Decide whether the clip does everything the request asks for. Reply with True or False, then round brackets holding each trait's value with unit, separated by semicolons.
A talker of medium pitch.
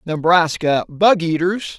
True (170 Hz)